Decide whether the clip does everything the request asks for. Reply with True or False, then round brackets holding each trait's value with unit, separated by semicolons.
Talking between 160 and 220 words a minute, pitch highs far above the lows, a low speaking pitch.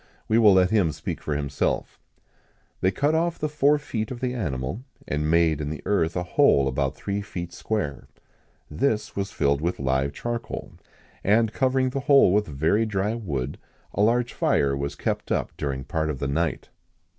True (180 wpm; 8.0 semitones; 95 Hz)